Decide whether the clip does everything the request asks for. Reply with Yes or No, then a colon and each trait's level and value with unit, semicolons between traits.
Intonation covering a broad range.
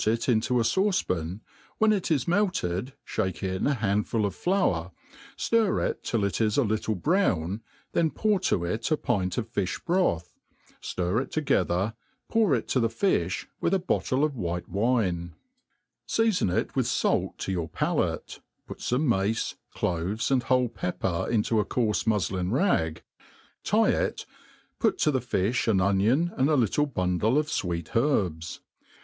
Yes: wide, 7.5 semitones